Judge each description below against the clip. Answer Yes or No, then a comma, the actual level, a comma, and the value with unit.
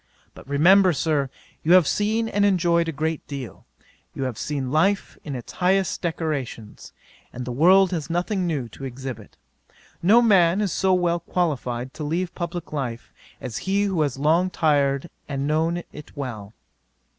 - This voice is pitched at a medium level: Yes, medium, 160 Hz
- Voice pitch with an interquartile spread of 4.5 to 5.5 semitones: Yes, average, 4.9 semitones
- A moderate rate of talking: Yes, average, 170 wpm